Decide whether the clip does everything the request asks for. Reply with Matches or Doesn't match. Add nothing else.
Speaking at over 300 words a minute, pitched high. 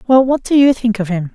Matches